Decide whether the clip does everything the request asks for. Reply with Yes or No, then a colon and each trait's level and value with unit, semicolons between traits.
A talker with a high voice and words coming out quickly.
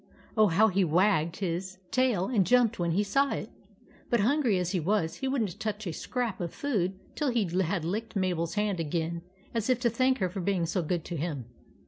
Yes: high, 195 Hz; fast, 220 wpm